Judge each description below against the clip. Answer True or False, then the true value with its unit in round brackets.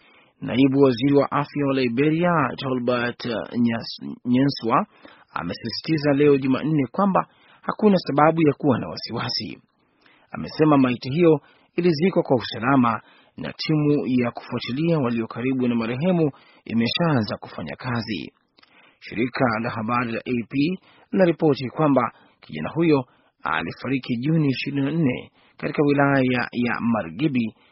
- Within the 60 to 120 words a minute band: True (110 wpm)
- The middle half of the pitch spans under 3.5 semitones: False (4.1 semitones)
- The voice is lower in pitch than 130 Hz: False (135 Hz)